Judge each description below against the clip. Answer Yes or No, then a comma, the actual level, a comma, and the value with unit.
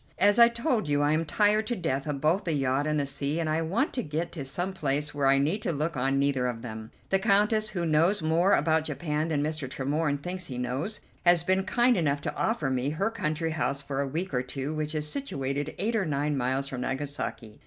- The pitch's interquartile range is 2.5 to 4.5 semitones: No, average, 4.9 semitones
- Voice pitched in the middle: Yes, medium, 155 Hz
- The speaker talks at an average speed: No, fast, 235 wpm